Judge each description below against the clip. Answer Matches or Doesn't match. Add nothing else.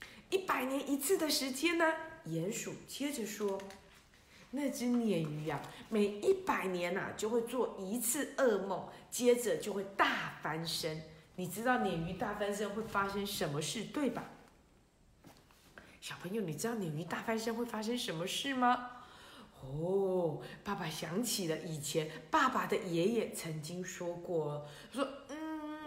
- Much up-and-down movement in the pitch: Matches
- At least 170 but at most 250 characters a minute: Matches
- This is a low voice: Doesn't match